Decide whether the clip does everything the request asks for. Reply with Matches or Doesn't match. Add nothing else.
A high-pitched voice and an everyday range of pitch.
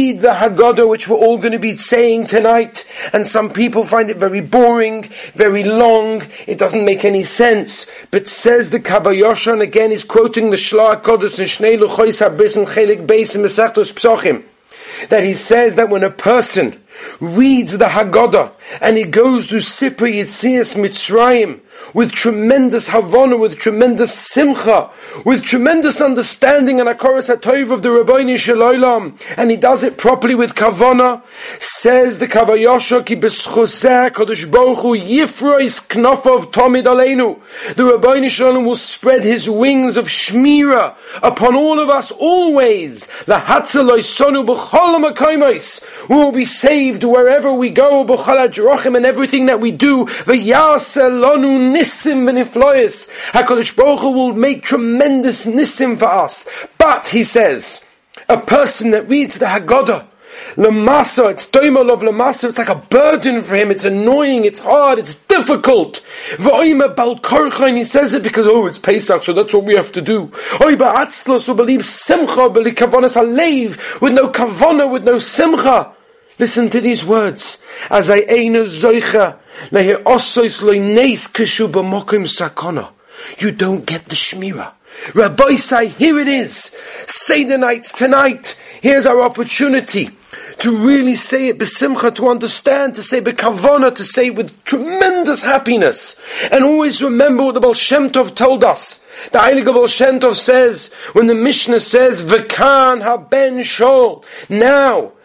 Matches